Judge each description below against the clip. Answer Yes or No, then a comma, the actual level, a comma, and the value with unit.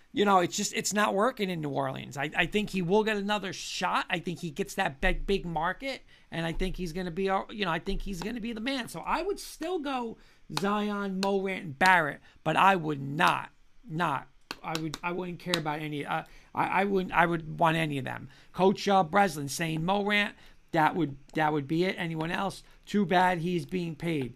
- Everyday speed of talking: No, fast, 230 wpm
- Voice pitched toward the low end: No, medium, 185 Hz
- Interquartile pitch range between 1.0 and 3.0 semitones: No, average, 3.7 semitones